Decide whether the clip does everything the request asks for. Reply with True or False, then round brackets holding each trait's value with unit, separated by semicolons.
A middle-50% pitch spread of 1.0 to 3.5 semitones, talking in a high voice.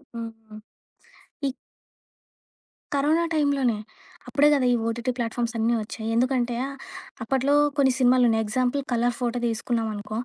True (2.7 semitones; 245 Hz)